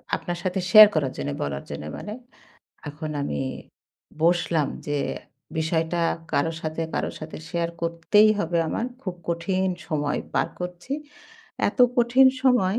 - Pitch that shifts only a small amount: No, average, 3.3 semitones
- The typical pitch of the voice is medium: Yes, medium, 170 Hz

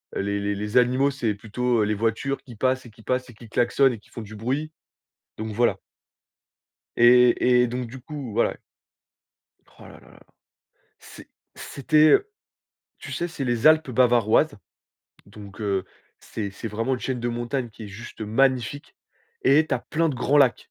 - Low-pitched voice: Yes, low, 120 Hz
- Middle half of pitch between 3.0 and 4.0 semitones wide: Yes, average, 3.4 semitones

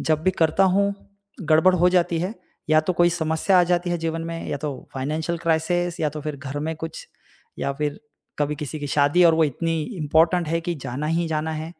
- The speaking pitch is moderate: Yes, medium, 160 Hz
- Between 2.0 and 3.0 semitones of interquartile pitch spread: Yes, narrow, 2.4 semitones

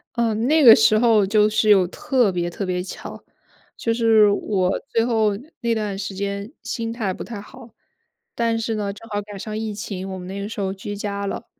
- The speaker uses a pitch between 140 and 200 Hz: No, high, 210 Hz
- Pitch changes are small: Yes, narrow, 2.3 semitones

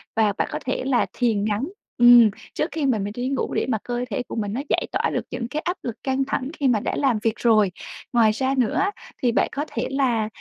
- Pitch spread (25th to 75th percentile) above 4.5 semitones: No, average, 3.4 semitones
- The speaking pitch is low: No, high, 245 Hz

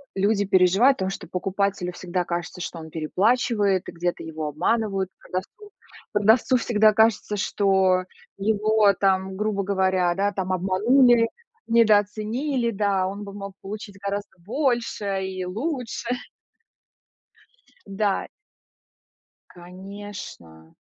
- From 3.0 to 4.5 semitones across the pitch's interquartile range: No, narrow, 2.6 semitones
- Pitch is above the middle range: Yes, high, 200 Hz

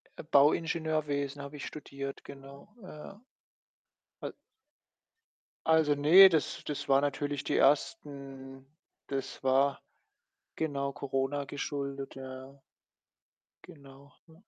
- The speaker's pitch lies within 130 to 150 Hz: Yes, medium, 140 Hz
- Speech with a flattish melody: Yes, narrow, 1.6 semitones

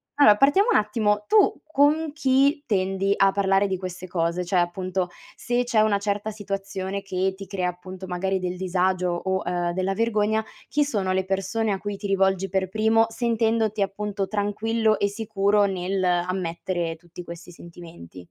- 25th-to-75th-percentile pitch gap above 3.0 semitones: No, average, 2.7 semitones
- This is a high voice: Yes, high, 195 Hz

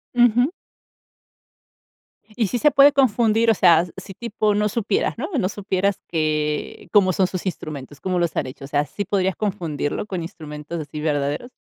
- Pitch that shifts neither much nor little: No, wide, 5.8 semitones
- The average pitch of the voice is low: No, medium, 185 Hz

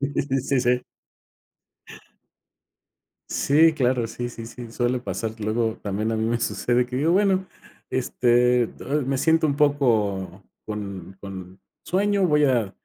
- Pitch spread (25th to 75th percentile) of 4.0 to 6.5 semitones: Yes, average, 4.5 semitones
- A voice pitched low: Yes, low, 125 Hz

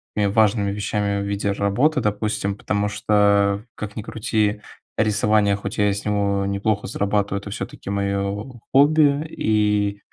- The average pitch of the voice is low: Yes, low, 105 Hz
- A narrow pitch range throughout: Yes, narrow, 1.1 semitones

